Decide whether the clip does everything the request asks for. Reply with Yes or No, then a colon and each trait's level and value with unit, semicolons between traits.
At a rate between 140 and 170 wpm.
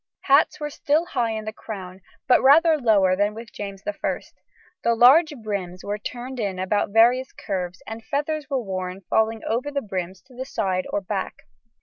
No: average, 185 wpm